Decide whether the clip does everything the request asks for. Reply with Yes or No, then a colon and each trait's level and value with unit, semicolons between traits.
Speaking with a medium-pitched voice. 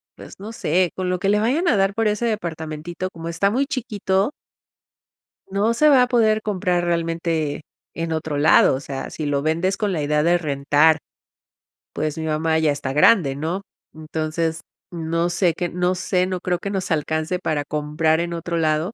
Yes: medium, 170 Hz